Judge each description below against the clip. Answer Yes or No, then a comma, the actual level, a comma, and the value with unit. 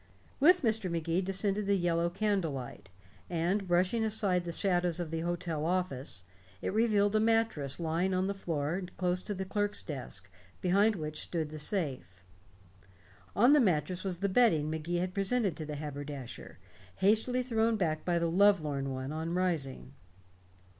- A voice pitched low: No, medium, 180 Hz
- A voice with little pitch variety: No, average, 4.5 semitones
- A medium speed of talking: Yes, average, 160 wpm